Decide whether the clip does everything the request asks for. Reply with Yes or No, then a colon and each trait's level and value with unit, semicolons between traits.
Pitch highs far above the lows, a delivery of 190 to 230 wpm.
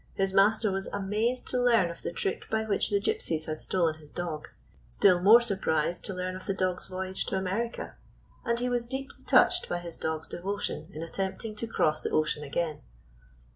No: average, 4.5 semitones; average, 195 wpm